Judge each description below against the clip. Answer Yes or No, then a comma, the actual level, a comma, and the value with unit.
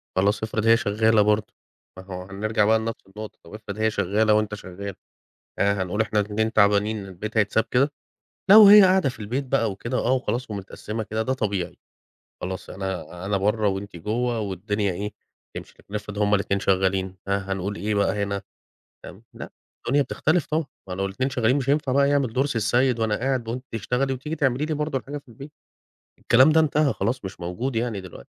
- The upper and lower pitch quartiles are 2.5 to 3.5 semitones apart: No, average, 4.2 semitones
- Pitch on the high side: No, low, 110 Hz